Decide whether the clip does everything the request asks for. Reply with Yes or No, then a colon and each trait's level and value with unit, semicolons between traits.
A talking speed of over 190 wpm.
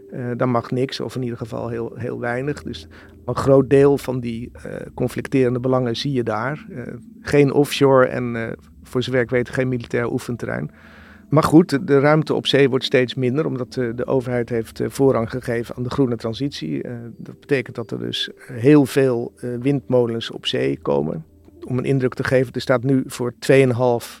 Yes: fast, 200 wpm